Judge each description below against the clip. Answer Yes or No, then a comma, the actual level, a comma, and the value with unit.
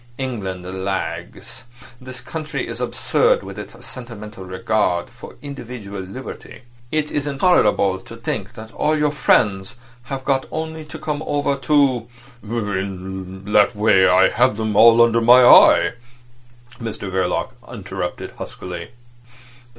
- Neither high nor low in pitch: No, low, 115 Hz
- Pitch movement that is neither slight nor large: No, wide, 6.0 semitones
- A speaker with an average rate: No, slow, 125 wpm